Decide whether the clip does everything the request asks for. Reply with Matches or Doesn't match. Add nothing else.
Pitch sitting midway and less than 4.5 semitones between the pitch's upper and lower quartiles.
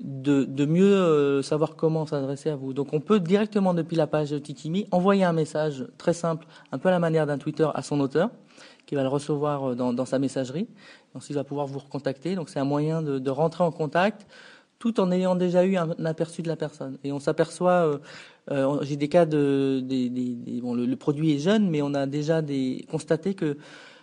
Matches